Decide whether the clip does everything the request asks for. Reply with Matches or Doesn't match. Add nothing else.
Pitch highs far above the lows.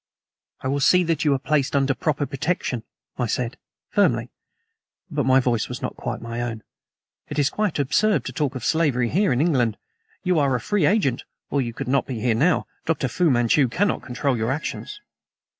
Doesn't match